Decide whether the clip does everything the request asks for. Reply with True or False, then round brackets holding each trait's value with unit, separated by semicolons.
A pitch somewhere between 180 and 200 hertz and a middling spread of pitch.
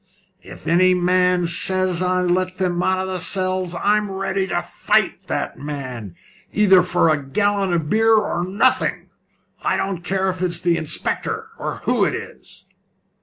False (185 Hz; 1.9 semitones)